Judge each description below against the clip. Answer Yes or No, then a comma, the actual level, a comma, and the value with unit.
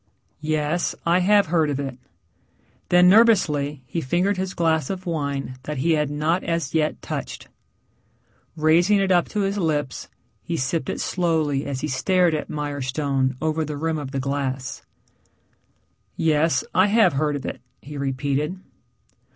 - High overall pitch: No, medium, 155 Hz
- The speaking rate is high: No, average, 155 wpm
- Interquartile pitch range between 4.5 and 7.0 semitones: No, average, 3.8 semitones